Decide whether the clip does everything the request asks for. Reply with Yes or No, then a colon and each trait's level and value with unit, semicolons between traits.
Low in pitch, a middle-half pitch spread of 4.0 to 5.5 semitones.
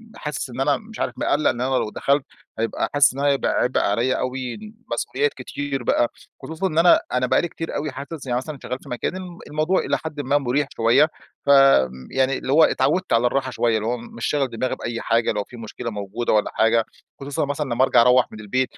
No: low, 130 Hz; average, 3.4 semitones